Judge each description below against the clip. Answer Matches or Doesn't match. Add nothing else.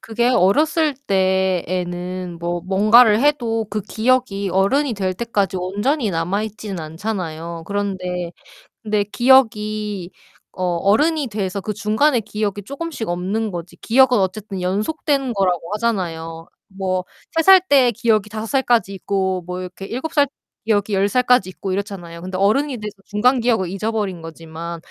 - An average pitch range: Matches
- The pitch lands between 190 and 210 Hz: Matches